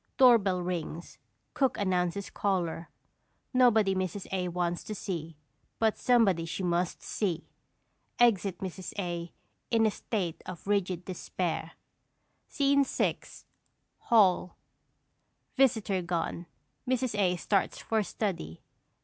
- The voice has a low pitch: No, medium, 185 Hz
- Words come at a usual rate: No, slow, 110 wpm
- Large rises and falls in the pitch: No, average, 3.8 semitones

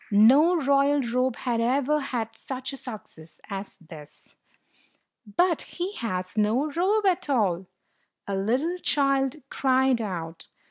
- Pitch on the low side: No, very high, 255 Hz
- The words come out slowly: Yes, slow, 130 wpm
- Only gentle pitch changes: No, average, 5.3 semitones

